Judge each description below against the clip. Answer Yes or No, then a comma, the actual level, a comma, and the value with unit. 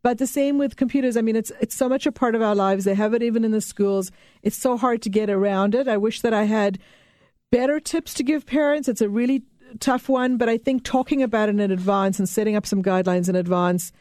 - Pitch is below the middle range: No, high, 225 Hz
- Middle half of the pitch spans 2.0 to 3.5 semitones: No, average, 4.3 semitones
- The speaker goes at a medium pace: No, fast, 255 wpm